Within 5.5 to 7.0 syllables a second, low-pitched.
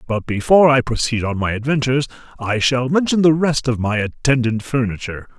Yes: 5.8 syllables/s; low, 125 Hz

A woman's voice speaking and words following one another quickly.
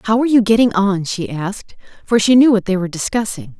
Yes: female; fast, 235 wpm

